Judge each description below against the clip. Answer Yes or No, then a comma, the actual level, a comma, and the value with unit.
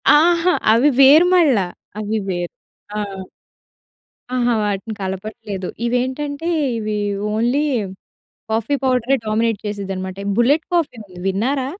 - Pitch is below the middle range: No, high, 230 Hz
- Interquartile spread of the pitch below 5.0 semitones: No, wide, 5.5 semitones